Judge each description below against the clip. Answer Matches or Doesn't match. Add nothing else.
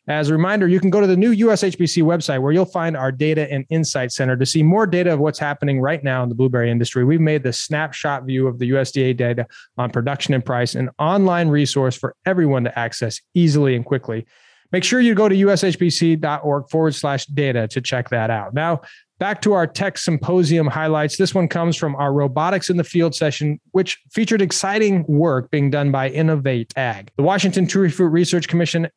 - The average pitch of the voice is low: Doesn't match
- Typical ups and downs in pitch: Matches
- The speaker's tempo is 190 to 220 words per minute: Matches